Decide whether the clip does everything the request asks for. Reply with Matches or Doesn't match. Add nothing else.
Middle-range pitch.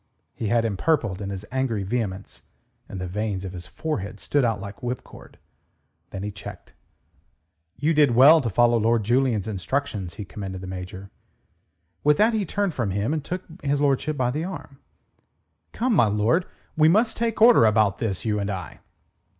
Doesn't match